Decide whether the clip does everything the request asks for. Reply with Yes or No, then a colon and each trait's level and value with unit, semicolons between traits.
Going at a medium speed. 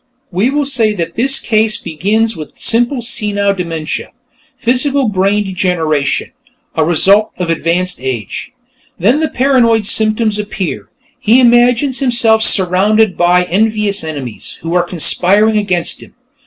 No: slow, 130 wpm